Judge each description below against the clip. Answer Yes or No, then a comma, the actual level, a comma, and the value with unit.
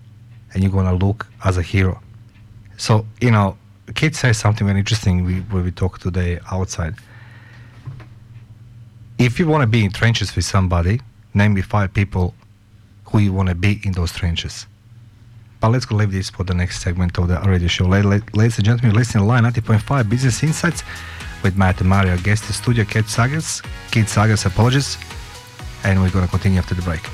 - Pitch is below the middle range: Yes, low, 105 Hz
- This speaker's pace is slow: No, average, 175 wpm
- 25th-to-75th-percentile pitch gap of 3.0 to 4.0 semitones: Yes, average, 3.4 semitones